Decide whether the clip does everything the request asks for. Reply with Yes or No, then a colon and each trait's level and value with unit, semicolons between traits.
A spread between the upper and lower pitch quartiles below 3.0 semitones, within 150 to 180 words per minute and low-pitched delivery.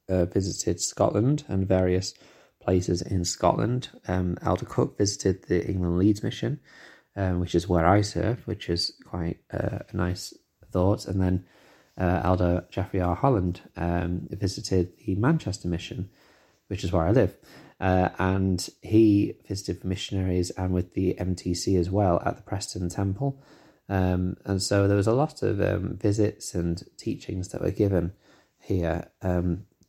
Yes: narrow, 2.5 semitones; average, 160 wpm; very low, 95 Hz